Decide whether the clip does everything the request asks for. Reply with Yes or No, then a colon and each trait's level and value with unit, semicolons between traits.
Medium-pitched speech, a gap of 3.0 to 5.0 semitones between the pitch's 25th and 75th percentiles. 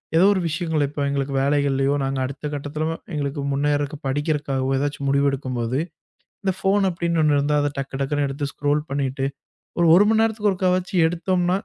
Yes: medium, 145 Hz; average, 3.6 semitones